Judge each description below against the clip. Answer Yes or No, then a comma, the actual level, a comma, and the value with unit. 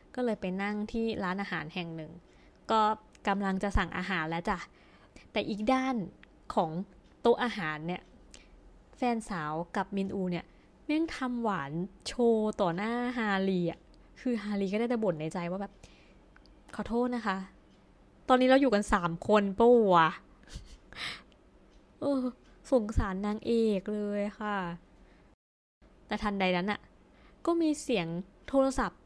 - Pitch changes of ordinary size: Yes, average, 4.3 semitones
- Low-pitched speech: No, high, 205 Hz